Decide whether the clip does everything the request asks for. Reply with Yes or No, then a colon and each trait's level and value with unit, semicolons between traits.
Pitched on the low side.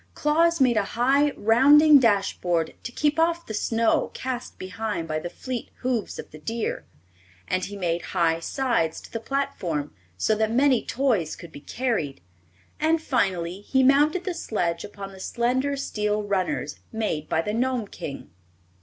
No: high, 225 Hz